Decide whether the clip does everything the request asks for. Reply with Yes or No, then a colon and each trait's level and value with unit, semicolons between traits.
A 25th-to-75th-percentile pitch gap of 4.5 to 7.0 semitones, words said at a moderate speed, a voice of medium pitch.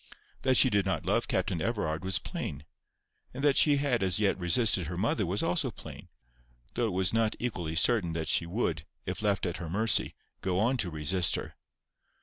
No: average, 4.8 semitones; average, 195 wpm; very low, 95 Hz